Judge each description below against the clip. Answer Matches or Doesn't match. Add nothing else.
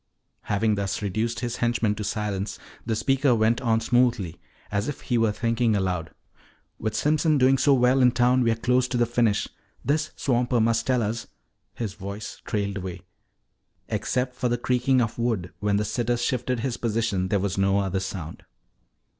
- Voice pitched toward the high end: Doesn't match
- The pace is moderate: Matches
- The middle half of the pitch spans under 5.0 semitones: Matches